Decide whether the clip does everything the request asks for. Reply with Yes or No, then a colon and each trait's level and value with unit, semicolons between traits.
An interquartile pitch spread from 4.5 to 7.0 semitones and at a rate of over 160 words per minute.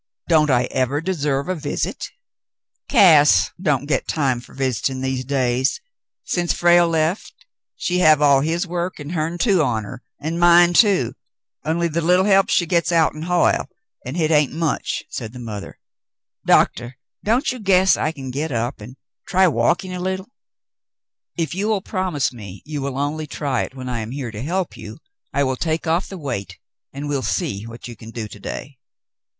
Yes: average, 5.1 semitones; average, 190 wpm